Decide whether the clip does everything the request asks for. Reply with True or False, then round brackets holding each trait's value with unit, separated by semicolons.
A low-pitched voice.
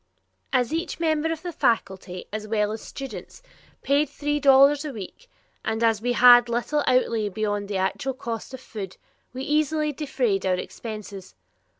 False (245 Hz)